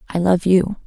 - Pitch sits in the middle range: Yes, medium, 180 Hz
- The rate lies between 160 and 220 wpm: Yes, fast, 210 wpm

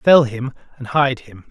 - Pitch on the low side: Yes, low, 130 Hz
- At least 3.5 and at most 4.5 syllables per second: Yes, 4.1 syllables/s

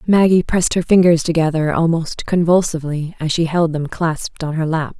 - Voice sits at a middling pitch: Yes, medium, 165 Hz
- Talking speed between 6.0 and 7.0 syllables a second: No, 5.4 syllables/s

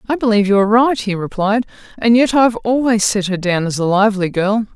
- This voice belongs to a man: No, female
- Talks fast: Yes, fast, 240 wpm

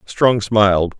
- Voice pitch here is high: No, low, 105 Hz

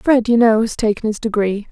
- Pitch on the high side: Yes, high, 220 Hz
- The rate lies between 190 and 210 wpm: No, fast, 245 wpm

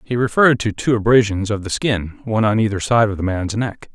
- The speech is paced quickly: Yes, fast, 230 wpm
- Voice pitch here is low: Yes, low, 110 Hz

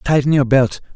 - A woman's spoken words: No, male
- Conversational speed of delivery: Yes, average, 190 wpm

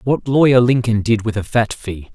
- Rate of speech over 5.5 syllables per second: No, 4.9 syllables/s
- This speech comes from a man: Yes, male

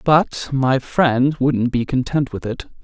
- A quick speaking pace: No, average, 170 wpm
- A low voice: Yes, low, 130 Hz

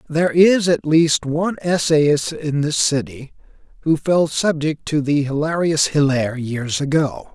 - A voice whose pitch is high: No, medium, 150 Hz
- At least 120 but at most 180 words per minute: Yes, average, 145 wpm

